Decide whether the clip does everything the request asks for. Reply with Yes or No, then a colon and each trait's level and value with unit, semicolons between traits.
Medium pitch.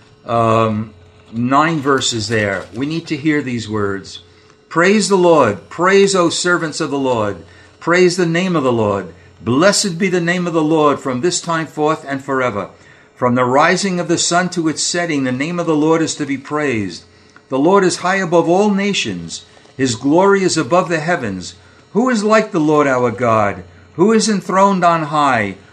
Yes: medium, 150 Hz